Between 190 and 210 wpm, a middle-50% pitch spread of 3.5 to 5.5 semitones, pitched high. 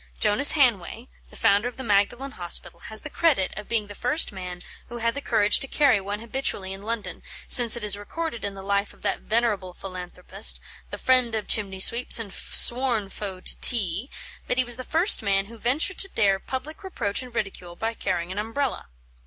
Yes: average, 200 wpm; average, 4.1 semitones; high, 220 Hz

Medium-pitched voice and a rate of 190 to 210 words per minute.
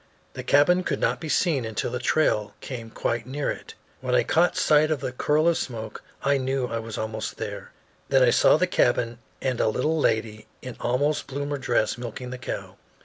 No: low, 130 Hz; average, 200 wpm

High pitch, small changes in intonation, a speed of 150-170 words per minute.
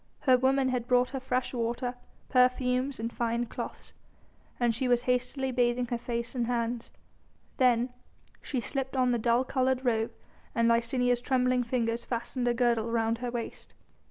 Yes: high, 245 Hz; narrow, 1.4 semitones; average, 160 wpm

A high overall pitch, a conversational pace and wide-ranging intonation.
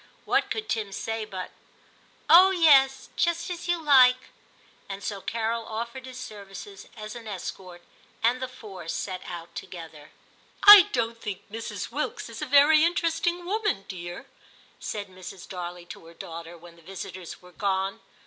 Yes: high, 215 Hz; average, 170 wpm; wide, 6.5 semitones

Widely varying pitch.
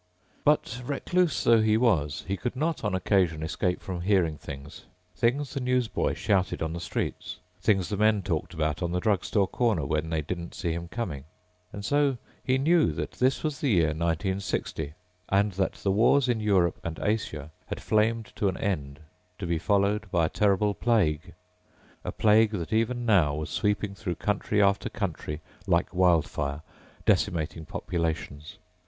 No: average, 5.0 semitones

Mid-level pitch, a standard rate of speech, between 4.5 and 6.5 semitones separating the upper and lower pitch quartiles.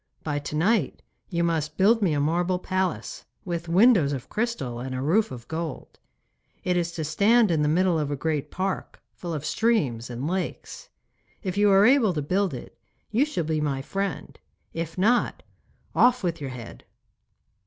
Yes: medium, 170 Hz; average, 180 wpm; average, 4.8 semitones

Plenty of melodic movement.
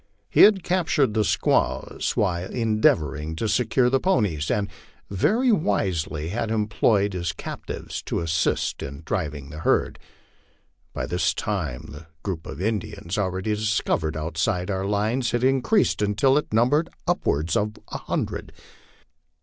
Yes: wide, 6.0 semitones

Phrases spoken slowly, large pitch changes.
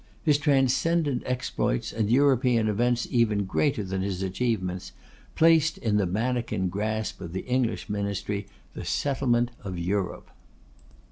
No: slow, 130 wpm; average, 4.7 semitones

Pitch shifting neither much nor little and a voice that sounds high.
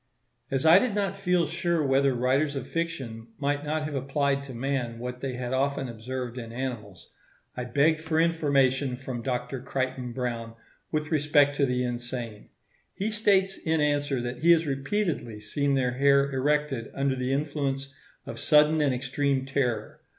No: average, 3.2 semitones; low, 135 Hz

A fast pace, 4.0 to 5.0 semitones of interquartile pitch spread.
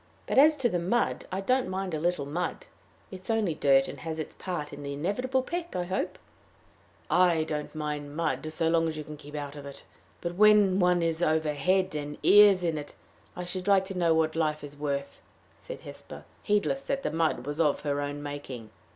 Yes: fast, 215 wpm; average, 4.4 semitones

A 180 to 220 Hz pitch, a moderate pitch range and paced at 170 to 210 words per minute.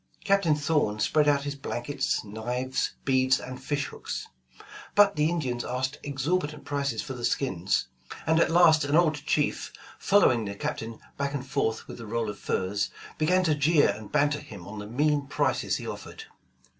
No: medium, 140 Hz; average, 4.1 semitones; average, 175 wpm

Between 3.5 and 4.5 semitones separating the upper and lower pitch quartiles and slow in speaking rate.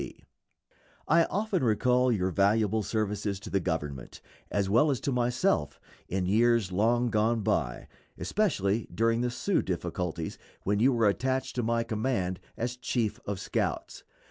No: average, 4.0 semitones; average, 150 wpm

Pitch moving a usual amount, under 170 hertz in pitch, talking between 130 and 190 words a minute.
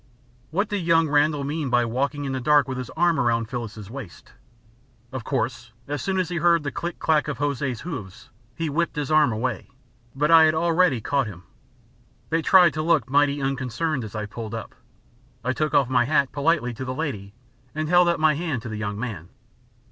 No: average, 4.7 semitones; medium, 140 Hz; fast, 205 wpm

